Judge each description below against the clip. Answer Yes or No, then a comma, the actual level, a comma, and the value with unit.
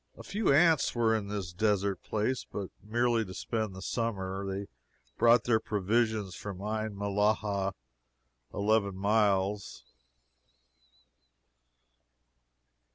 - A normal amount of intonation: No, narrow, 2.2 semitones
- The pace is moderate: No, slow, 105 wpm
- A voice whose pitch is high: No, low, 105 Hz